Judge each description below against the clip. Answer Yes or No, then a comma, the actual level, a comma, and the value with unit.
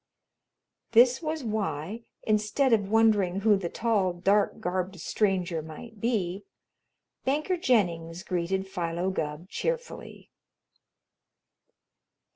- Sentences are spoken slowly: Yes, slow, 95 wpm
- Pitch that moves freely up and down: No, average, 4.2 semitones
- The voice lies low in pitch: No, high, 195 Hz